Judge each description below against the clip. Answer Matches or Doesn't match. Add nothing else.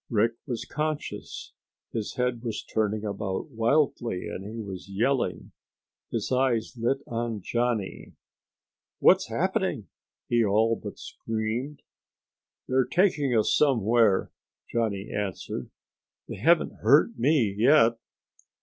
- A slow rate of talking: Matches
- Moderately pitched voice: Doesn't match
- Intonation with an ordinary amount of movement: Matches